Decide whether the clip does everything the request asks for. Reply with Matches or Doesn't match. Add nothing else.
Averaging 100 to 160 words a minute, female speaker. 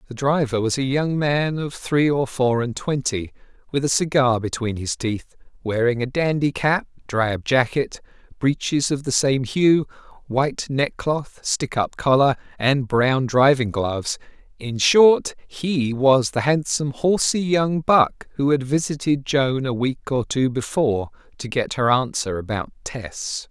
Doesn't match